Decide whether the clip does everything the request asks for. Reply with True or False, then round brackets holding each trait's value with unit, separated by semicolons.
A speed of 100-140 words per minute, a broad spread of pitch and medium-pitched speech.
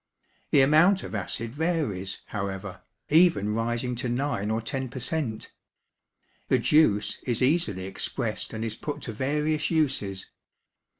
False (135 wpm; 6.0 semitones; 120 Hz)